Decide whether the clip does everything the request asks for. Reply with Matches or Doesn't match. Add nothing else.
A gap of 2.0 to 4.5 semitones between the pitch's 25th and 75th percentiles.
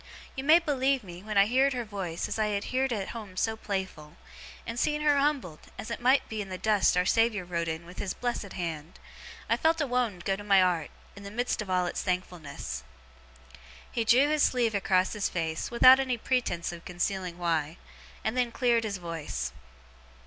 Doesn't match